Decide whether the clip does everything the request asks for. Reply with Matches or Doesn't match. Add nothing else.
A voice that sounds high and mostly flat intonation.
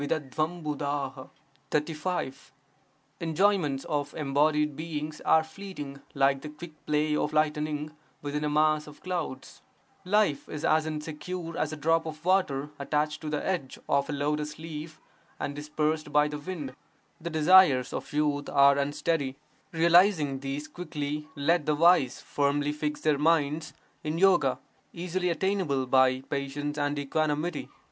Doesn't match